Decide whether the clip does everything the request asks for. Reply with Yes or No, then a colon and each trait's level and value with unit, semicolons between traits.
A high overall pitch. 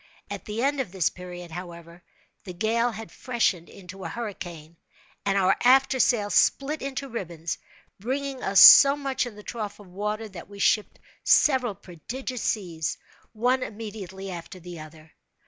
Yes: high, 205 Hz